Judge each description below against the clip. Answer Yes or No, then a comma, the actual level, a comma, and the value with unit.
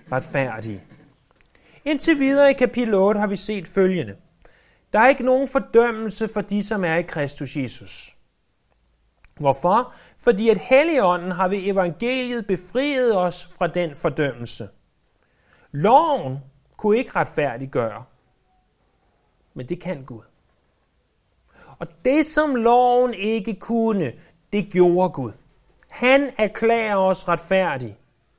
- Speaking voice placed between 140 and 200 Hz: Yes, medium, 185 Hz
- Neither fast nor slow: No, slow, 115 wpm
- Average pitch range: No, wide, 8.8 semitones